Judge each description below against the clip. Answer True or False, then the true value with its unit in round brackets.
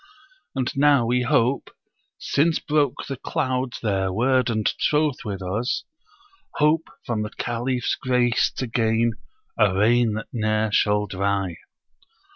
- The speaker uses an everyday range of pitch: True (3.3 semitones)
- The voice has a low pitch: True (120 Hz)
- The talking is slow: True (130 wpm)